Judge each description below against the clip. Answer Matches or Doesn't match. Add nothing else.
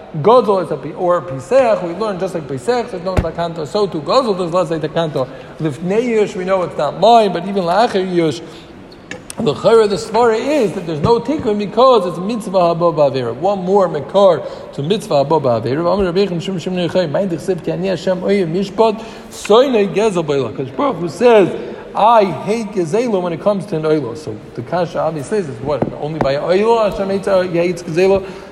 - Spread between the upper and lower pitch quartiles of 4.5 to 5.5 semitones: Doesn't match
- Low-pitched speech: Doesn't match